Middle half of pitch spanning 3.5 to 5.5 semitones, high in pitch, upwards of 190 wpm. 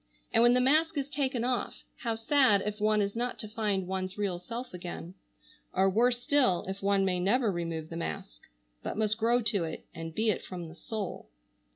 Yes: average, 4.8 semitones; high, 210 Hz; fast, 205 wpm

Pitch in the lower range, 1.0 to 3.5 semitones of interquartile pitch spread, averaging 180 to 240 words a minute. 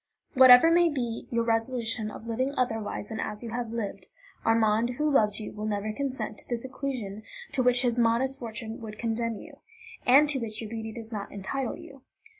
No: high, 230 Hz; average, 2.7 semitones; average, 195 wpm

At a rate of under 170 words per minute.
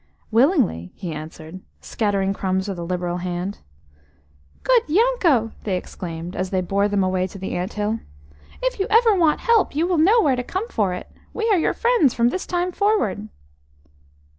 No: average, 180 wpm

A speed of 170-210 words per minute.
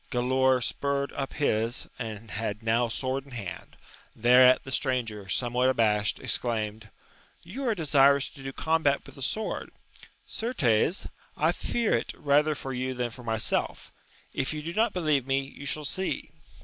No: average, 160 wpm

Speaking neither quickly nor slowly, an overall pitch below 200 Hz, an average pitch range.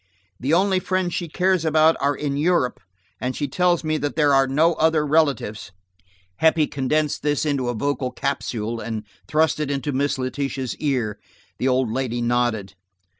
Yes: average, 165 wpm; medium, 140 Hz; average, 3.6 semitones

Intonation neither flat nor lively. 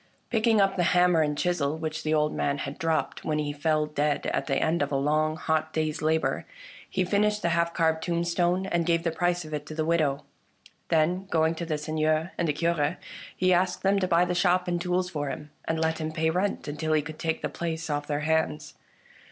No: narrow, 2.3 semitones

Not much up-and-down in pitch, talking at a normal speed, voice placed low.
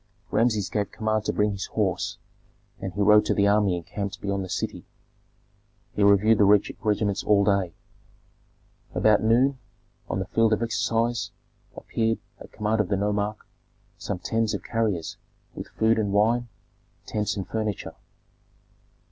Yes: narrow, 1.8 semitones; average, 150 wpm; low, 105 Hz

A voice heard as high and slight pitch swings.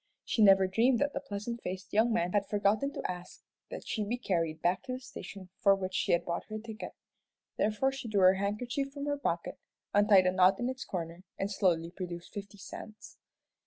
No: high, 200 Hz; average, 4.0 semitones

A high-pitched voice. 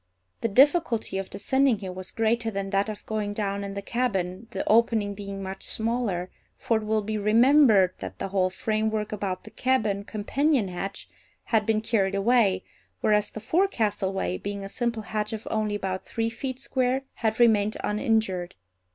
Yes: high, 215 Hz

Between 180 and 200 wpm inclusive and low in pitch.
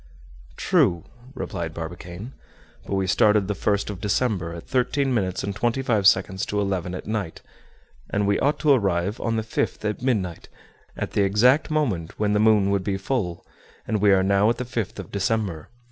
Yes: average, 190 wpm; low, 100 Hz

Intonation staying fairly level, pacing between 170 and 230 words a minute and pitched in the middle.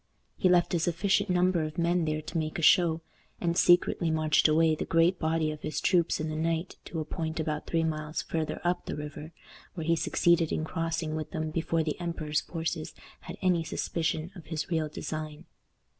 Yes: narrow, 1.6 semitones; average, 200 wpm; medium, 160 Hz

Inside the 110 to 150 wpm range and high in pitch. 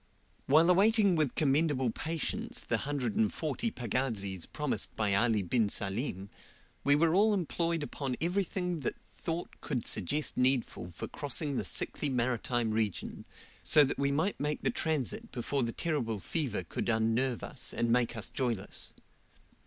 No: average, 145 wpm; low, 135 Hz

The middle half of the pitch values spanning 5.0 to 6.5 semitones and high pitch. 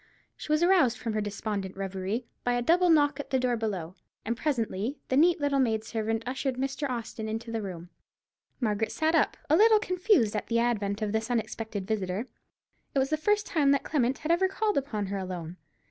Yes: wide, 5.6 semitones; high, 235 Hz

